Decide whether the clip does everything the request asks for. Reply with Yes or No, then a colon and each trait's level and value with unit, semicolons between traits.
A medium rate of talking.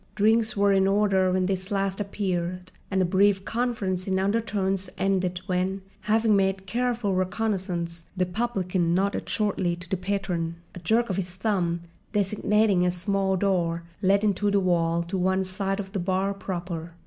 Yes: average, 165 wpm